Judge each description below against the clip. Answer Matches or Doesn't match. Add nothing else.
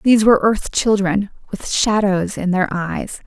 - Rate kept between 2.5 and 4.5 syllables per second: Matches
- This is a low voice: Doesn't match